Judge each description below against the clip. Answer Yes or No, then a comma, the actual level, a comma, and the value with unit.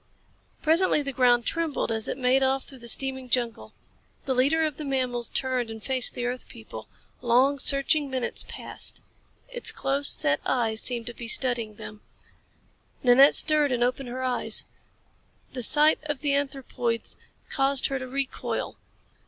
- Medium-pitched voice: No, very high, 260 Hz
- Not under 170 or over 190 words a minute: No, average, 160 wpm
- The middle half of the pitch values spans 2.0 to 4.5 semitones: Yes, narrow, 2.4 semitones